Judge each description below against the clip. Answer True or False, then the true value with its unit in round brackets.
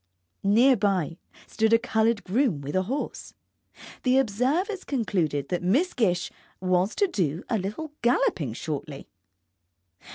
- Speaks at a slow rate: True (130 wpm)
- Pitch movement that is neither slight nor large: False (6.2 semitones)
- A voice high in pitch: True (210 Hz)